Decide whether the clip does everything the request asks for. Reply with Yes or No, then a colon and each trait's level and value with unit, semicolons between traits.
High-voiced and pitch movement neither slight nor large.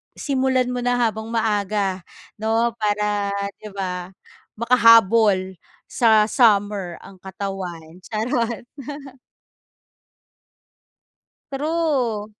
Yes: high, 215 Hz; average, 3.1 semitones